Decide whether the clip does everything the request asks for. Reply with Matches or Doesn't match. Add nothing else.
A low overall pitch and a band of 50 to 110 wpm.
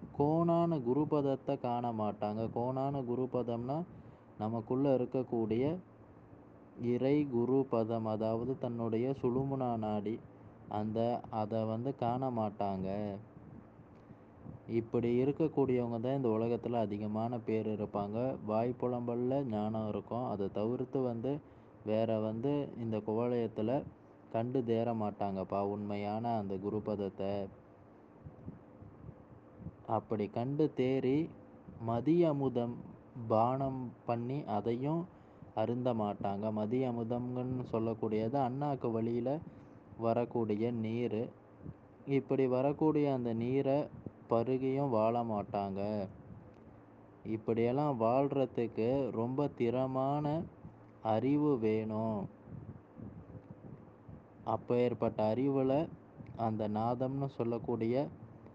Matches